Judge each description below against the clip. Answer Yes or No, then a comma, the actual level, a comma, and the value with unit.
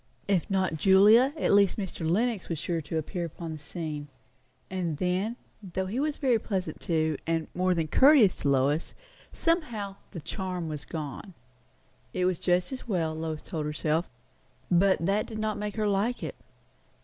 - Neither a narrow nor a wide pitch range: Yes, average, 4.4 semitones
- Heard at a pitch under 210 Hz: Yes, medium, 185 Hz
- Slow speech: No, average, 175 wpm